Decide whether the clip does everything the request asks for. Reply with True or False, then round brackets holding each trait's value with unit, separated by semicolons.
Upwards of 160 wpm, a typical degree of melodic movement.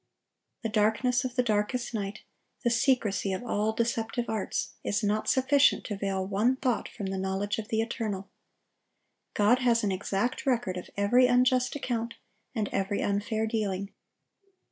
False (155 wpm; 3.3 semitones)